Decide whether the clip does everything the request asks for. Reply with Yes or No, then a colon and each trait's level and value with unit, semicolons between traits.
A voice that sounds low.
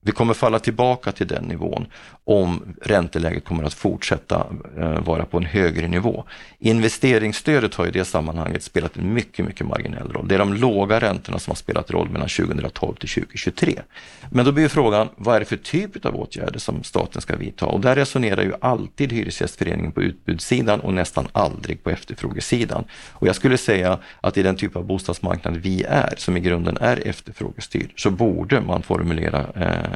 Yes: very low, 95 Hz